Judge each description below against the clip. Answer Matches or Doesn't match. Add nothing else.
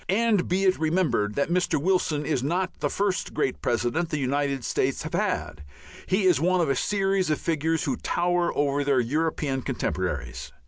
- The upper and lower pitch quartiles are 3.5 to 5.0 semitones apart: Matches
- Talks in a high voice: Doesn't match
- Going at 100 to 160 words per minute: Doesn't match